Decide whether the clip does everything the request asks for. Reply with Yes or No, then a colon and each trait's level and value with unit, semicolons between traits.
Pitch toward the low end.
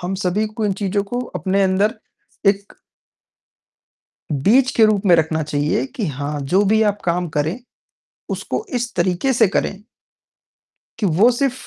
No: high, 195 Hz